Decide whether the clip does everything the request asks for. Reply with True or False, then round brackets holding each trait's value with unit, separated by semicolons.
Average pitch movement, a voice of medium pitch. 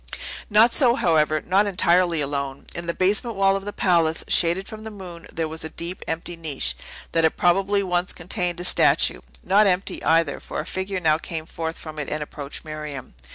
True (3.4 semitones; 170 Hz)